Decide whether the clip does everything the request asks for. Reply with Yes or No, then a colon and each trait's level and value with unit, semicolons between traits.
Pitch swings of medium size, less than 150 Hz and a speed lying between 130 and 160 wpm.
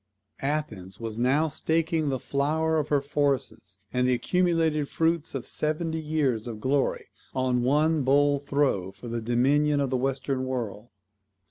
Yes: average, 3.4 semitones; medium, 140 Hz; average, 150 wpm